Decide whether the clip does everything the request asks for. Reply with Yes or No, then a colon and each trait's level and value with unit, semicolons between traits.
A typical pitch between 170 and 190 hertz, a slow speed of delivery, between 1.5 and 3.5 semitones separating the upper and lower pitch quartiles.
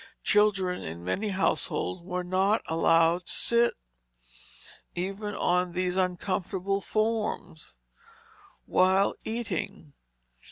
Yes: medium, 185 Hz; slow, 90 wpm; narrow, 2.6 semitones